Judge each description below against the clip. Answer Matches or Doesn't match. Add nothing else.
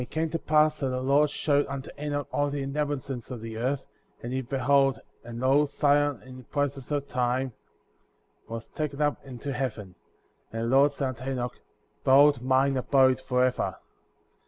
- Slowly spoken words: Doesn't match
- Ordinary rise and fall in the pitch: Doesn't match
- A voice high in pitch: Doesn't match